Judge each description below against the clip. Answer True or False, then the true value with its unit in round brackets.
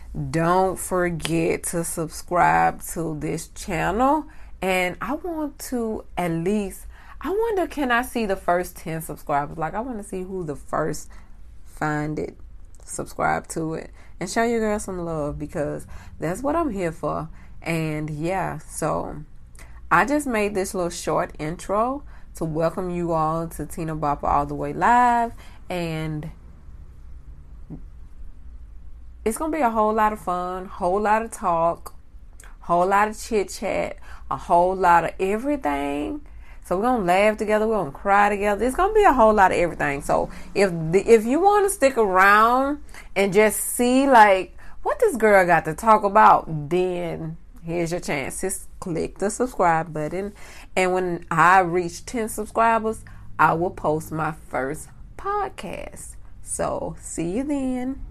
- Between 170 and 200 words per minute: False (160 wpm)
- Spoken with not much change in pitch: False (5.6 semitones)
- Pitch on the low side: False (180 Hz)